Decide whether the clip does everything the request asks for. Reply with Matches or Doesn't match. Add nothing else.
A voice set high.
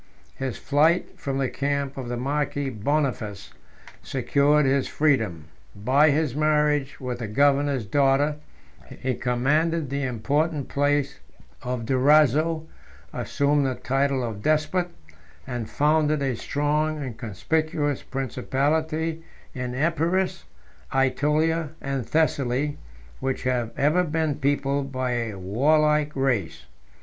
Doesn't match